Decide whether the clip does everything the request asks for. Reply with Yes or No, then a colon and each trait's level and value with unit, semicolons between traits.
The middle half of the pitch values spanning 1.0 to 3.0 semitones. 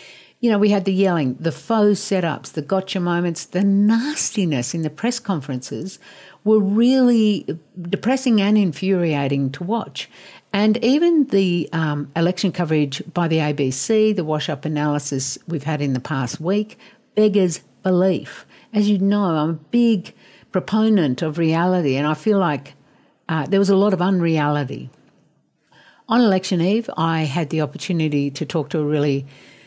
No: average, 5.2 semitones